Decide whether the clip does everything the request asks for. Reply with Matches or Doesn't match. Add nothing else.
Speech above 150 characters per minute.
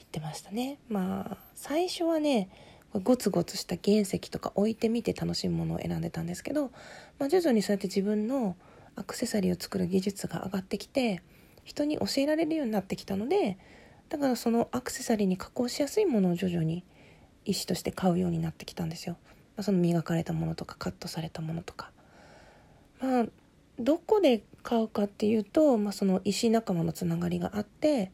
Matches